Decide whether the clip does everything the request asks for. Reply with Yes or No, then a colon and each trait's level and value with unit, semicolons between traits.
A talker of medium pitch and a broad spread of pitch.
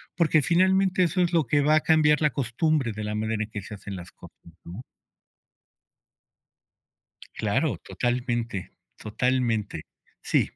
No: low, 125 Hz; wide, 6.6 semitones